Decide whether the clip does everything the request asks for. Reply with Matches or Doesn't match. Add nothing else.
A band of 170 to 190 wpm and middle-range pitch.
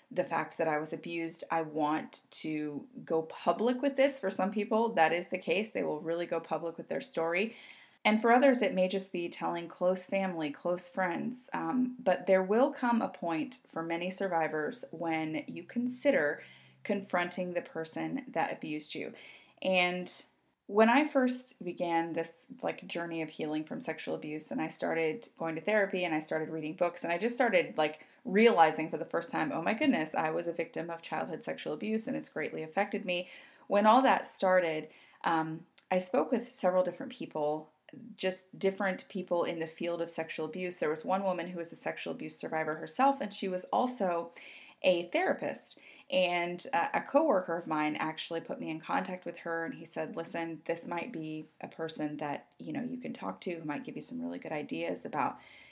Doesn't match